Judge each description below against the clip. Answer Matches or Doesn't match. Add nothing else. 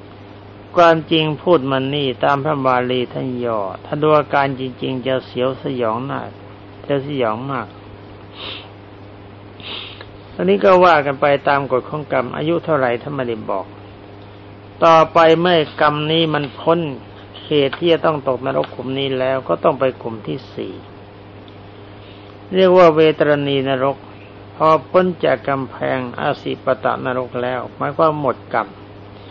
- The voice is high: Doesn't match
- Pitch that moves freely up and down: Matches